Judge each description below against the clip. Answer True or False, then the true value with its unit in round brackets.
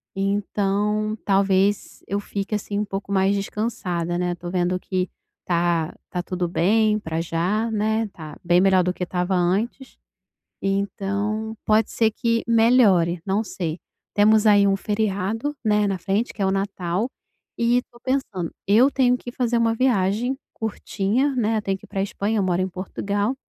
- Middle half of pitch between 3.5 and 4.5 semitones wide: False (3.0 semitones)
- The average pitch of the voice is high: True (200 Hz)